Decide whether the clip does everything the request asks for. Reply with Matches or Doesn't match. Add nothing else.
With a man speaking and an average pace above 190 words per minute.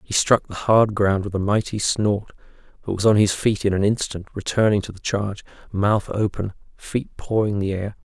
Matches